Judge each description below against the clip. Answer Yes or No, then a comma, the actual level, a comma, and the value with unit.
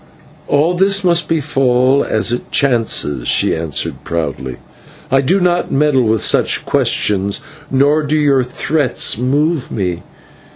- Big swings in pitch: Yes, wide, 6.0 semitones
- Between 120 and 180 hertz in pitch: Yes, low, 135 Hz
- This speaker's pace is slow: Yes, slow, 130 wpm